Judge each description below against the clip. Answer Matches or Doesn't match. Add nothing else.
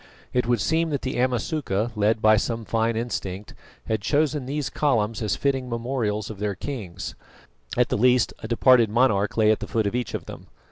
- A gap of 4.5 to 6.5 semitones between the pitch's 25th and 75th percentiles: Doesn't match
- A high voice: Doesn't match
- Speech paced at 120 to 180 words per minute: Doesn't match